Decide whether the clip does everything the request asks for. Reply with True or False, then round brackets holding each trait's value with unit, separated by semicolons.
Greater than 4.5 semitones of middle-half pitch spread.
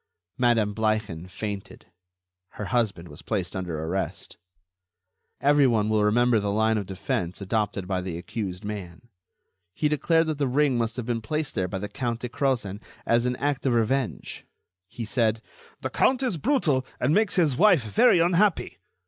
True (5.4 semitones)